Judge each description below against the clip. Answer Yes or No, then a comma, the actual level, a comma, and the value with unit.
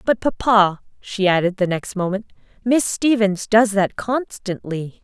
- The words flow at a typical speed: Yes, average, 145 wpm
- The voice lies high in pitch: Yes, high, 205 Hz